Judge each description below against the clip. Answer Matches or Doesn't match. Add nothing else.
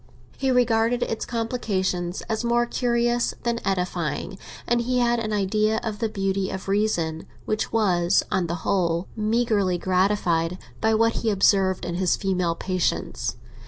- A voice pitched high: Matches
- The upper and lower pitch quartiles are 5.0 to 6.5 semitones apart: Doesn't match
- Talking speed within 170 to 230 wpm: Doesn't match